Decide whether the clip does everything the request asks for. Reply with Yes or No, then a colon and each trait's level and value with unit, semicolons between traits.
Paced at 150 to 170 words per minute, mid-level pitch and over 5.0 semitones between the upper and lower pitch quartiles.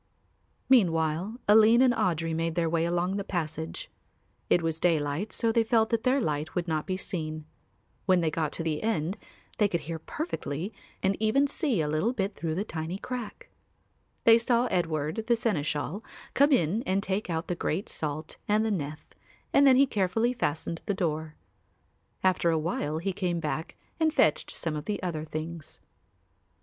No: average, 180 wpm; medium, 175 Hz; wide, 5.6 semitones